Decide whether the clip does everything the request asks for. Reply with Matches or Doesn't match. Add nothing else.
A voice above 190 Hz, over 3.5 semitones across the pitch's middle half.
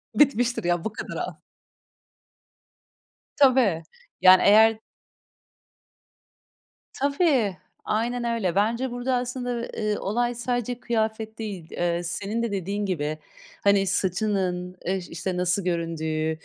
Matches